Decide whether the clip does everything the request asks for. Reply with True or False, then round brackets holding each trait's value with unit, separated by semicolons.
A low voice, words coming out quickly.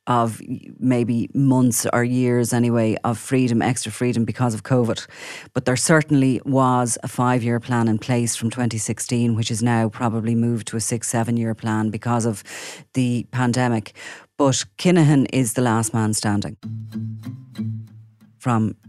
False (120 Hz; 155 wpm)